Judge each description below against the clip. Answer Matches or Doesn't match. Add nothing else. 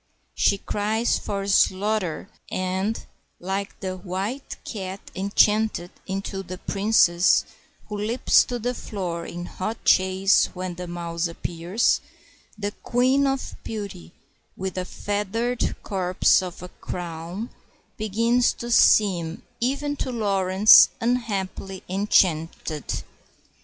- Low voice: Doesn't match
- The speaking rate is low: Matches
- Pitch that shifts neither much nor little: Matches